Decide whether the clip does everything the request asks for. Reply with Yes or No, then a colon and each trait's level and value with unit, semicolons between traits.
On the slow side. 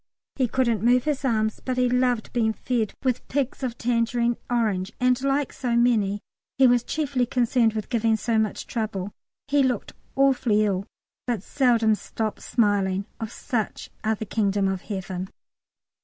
No: average, 160 wpm